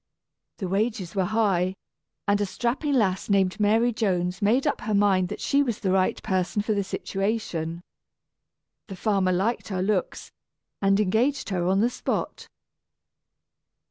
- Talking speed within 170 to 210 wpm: No, average, 150 wpm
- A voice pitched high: Yes, high, 200 Hz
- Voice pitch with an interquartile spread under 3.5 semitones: Yes, average, 2.8 semitones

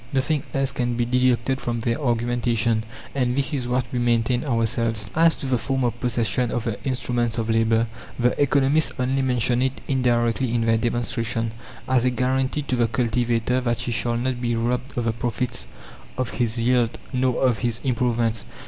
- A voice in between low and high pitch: No, low, 120 Hz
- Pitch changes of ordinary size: No, narrow, 1.8 semitones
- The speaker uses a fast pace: No, average, 185 wpm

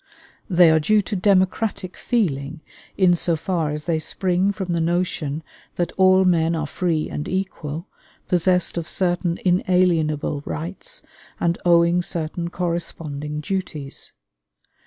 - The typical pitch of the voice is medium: Yes, medium, 175 Hz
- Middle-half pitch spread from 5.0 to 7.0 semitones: No, average, 2.7 semitones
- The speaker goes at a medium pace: No, slow, 130 wpm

